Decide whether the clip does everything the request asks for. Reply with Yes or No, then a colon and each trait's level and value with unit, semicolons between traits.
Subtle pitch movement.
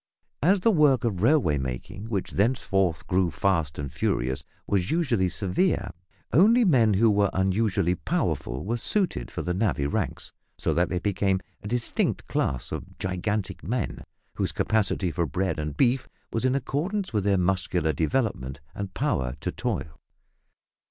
No: wide, 5.5 semitones